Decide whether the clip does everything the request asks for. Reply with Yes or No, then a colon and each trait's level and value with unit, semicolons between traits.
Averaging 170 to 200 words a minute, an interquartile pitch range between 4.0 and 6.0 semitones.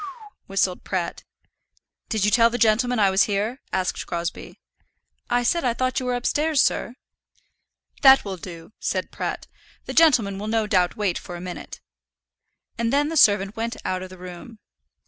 Yes: average, 185 wpm; average, 4.9 semitones